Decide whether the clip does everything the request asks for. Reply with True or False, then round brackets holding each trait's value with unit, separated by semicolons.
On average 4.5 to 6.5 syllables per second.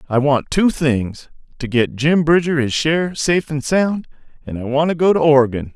True (5.1 syllables/s)